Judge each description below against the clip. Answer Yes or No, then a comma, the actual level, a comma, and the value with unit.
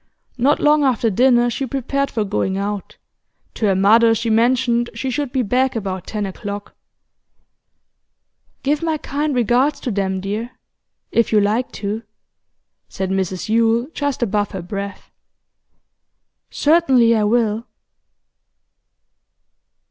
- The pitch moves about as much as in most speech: Yes, average, 4.2 semitones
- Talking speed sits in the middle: No, slow, 125 wpm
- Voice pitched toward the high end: Yes, high, 230 Hz